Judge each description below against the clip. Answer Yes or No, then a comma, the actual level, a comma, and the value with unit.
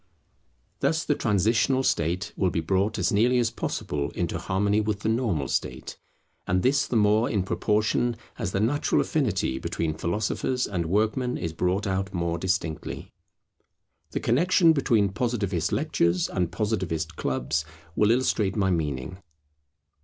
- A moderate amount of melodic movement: Yes, average, 5.0 semitones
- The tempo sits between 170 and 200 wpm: No, average, 145 wpm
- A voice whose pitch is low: Yes, low, 100 Hz